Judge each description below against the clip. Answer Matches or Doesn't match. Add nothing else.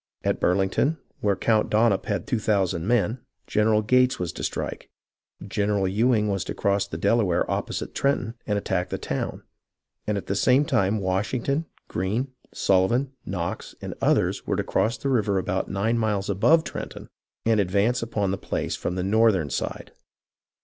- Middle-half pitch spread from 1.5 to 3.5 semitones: Matches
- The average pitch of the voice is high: Doesn't match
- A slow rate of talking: Doesn't match